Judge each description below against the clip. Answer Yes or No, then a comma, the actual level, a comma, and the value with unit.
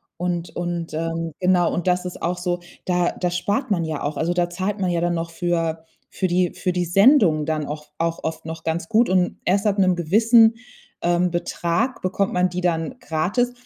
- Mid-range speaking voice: Yes, medium, 175 Hz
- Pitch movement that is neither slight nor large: No, narrow, 1.9 semitones